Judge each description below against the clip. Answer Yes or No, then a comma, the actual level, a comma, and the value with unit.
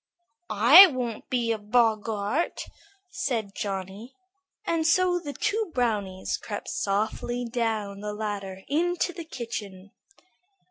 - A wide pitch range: Yes, wide, 5.9 semitones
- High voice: Yes, high, 230 Hz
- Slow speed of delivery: Yes, slow, 110 wpm